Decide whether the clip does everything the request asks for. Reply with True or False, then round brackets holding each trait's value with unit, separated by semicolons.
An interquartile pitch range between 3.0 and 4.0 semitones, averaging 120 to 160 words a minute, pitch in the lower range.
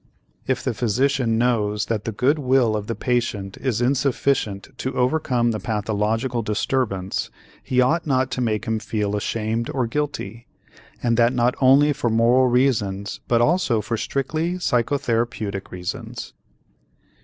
True (3.3 semitones; 145 wpm; 120 Hz)